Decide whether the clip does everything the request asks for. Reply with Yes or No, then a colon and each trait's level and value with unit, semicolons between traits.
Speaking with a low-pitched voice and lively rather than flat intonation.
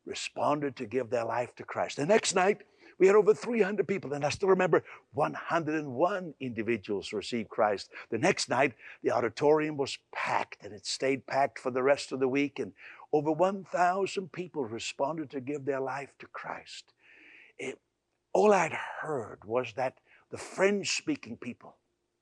No: medium, 150 Hz; wide, 6.0 semitones